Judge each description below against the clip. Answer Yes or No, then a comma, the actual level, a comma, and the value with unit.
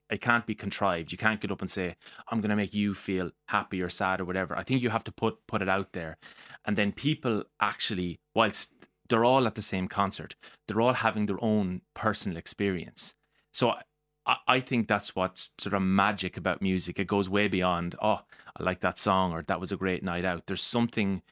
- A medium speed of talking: No, fast, 215 wpm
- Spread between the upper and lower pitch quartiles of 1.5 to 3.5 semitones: Yes, average, 2.9 semitones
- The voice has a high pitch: No, low, 100 Hz